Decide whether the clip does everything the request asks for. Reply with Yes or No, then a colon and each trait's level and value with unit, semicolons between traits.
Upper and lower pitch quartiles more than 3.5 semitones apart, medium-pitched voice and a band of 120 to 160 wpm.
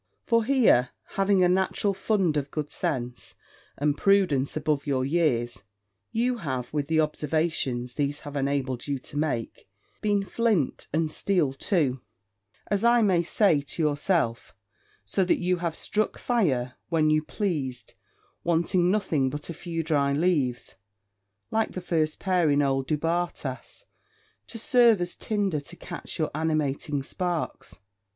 Yes: average, 5.0 semitones; medium, 155 Hz; average, 145 wpm